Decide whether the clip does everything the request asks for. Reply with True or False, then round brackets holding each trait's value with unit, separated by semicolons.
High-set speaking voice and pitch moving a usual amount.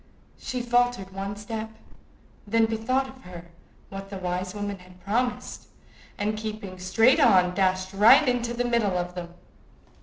True (205 Hz; 4.1 semitones)